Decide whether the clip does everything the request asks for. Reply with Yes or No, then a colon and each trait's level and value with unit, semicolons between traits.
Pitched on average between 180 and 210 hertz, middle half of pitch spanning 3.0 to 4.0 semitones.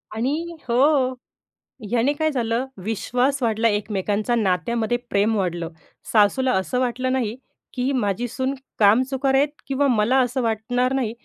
No: high, 240 Hz; average, 3.5 semitones